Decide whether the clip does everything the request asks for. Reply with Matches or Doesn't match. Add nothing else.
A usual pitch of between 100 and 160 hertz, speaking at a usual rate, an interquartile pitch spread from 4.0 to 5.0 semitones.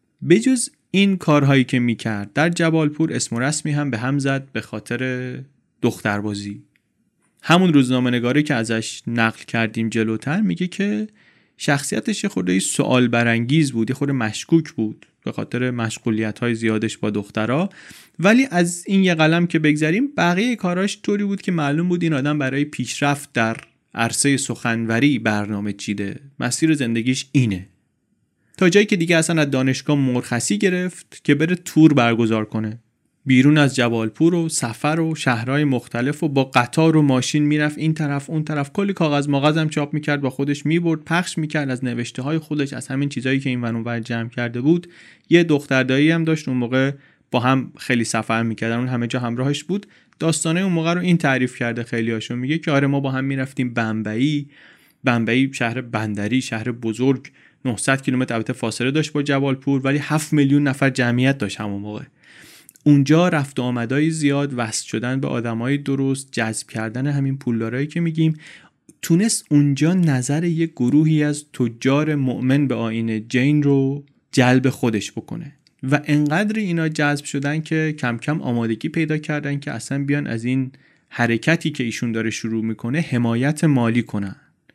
Doesn't match